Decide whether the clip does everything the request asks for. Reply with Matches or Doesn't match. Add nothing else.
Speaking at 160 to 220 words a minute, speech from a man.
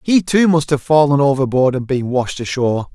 Matches